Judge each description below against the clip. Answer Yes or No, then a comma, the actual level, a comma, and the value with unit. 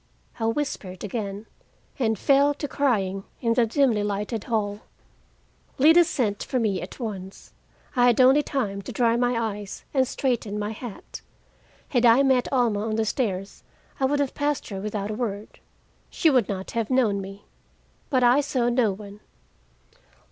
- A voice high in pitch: Yes, high, 230 Hz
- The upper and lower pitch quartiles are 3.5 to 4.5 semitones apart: Yes, average, 4.1 semitones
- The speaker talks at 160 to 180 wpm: Yes, average, 165 wpm